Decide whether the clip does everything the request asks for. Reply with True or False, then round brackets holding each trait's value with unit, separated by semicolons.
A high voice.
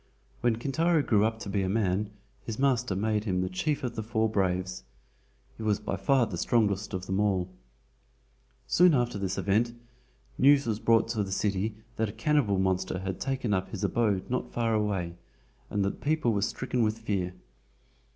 False (105 Hz)